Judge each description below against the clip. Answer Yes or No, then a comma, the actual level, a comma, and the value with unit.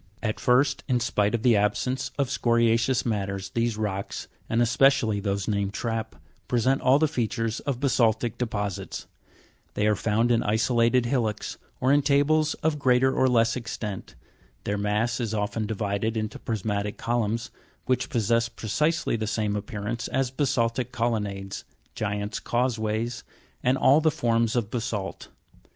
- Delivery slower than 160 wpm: Yes, average, 150 wpm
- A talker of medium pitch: No, low, 115 Hz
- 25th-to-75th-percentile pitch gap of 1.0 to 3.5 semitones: Yes, average, 2.9 semitones